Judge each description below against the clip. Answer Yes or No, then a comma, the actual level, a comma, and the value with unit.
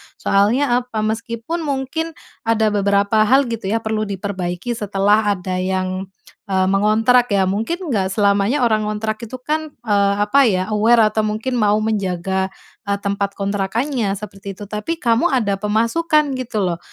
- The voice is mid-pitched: No, high, 215 Hz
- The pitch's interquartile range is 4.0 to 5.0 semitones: No, average, 3.3 semitones